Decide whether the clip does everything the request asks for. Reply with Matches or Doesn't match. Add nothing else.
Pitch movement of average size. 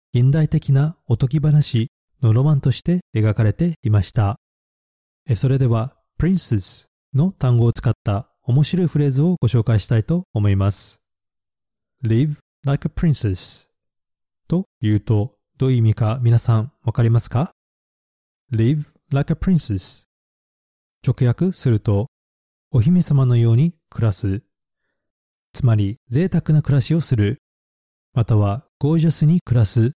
Doesn't match